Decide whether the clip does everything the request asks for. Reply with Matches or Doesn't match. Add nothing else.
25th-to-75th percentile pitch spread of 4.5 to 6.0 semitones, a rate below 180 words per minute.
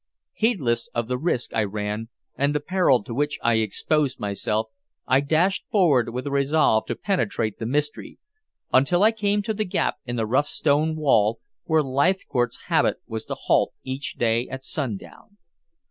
Matches